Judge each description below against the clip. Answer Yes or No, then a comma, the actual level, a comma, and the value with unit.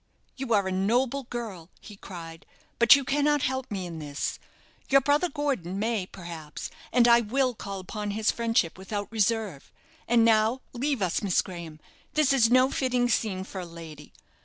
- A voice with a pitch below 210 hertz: No, high, 220 Hz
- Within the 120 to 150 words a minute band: No, average, 175 wpm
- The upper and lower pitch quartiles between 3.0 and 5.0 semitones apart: No, wide, 5.5 semitones